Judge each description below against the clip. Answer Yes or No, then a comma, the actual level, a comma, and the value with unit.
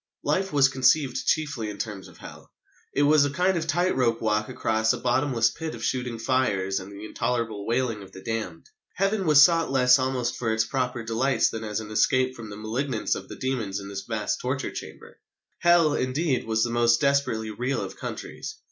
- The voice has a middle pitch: No, low, 125 Hz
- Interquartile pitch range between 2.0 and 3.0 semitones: No, average, 4.0 semitones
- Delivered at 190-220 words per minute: Yes, average, 200 wpm